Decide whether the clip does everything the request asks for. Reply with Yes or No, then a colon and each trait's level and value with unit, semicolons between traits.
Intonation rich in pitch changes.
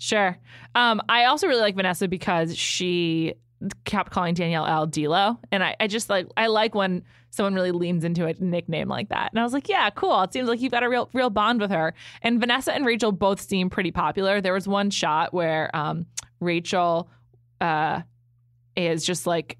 No: average, 4.4 semitones